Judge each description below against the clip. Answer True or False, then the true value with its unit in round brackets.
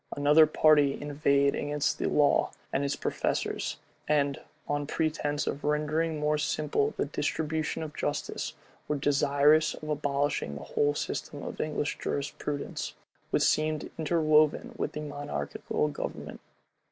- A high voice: False (150 Hz)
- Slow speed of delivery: True (130 wpm)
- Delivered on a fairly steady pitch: True (1.3 semitones)